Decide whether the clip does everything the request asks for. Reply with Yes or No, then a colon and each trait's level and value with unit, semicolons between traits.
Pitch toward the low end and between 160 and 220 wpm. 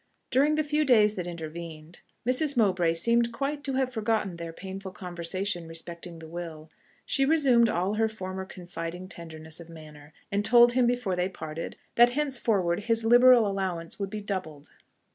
No: high, 190 Hz; average, 165 wpm